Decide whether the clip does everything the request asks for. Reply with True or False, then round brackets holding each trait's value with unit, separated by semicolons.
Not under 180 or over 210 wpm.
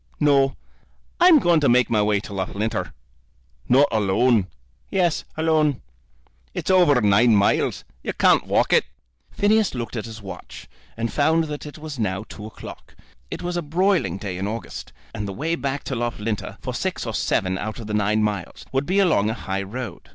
True (185 wpm)